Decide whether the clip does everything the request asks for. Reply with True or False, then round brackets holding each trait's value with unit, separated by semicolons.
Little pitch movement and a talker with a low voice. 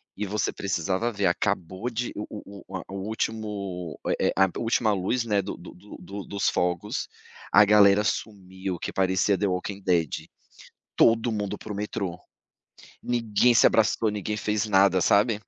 True (2.3 semitones; 100 Hz)